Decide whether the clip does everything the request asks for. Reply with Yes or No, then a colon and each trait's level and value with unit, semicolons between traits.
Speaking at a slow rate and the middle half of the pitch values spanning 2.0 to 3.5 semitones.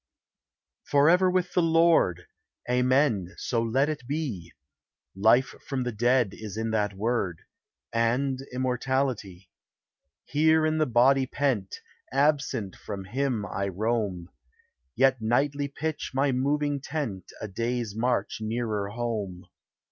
No: slow, 120 wpm; average, 4.7 semitones